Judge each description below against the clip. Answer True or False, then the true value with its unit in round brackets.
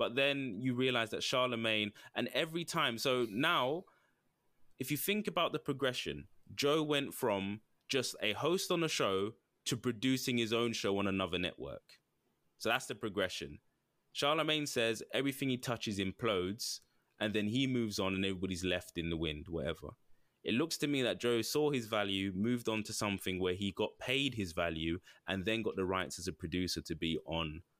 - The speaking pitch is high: False (110 Hz)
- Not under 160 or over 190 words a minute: True (185 wpm)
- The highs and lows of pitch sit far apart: True (6.0 semitones)